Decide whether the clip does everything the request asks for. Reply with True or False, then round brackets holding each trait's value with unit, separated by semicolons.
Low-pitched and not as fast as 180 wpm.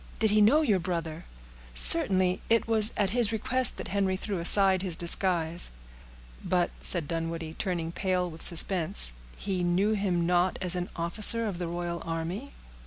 False (185 Hz; 165 wpm)